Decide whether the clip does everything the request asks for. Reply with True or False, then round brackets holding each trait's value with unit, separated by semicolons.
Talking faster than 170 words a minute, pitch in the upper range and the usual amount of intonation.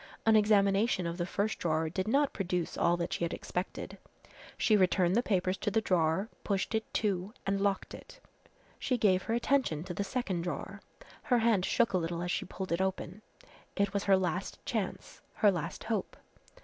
True (190 wpm; 195 Hz; 3.4 semitones)